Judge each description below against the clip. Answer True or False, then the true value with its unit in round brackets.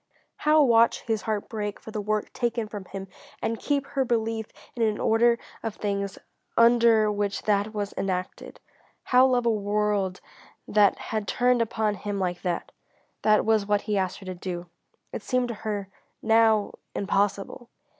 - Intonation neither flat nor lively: False (2.3 semitones)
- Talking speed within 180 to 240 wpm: False (165 wpm)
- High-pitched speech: True (215 Hz)